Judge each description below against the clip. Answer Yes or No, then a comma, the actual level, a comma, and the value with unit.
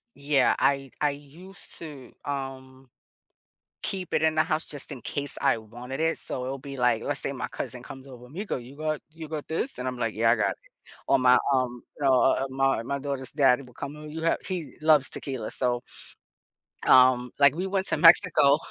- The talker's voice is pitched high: No, low, 135 Hz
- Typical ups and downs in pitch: Yes, average, 3.3 semitones